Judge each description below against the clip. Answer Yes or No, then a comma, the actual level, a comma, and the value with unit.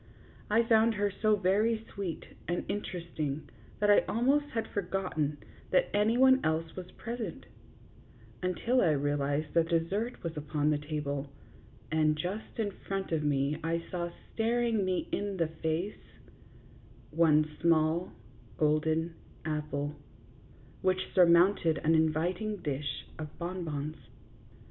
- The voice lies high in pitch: No, medium, 170 Hz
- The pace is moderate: No, slow, 130 wpm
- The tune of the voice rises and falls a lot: No, average, 5.0 semitones